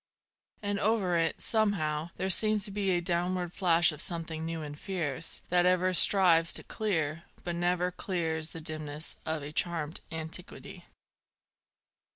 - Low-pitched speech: No, medium, 170 Hz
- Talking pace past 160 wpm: No, average, 150 wpm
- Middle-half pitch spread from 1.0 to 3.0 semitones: Yes, narrow, 2.5 semitones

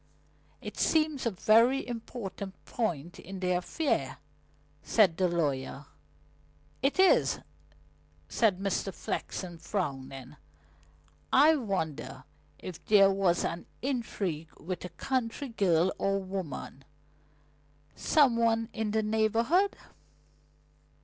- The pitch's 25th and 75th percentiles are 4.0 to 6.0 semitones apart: Yes, average, 5.2 semitones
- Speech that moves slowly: Yes, slow, 105 wpm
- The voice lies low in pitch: No, high, 195 Hz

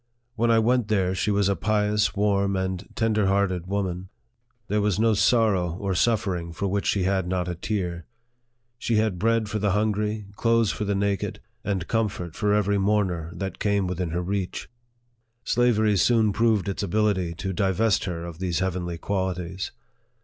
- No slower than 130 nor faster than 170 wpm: No, average, 180 wpm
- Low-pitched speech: Yes, low, 100 Hz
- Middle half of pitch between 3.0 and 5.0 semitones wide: No, narrow, 2.6 semitones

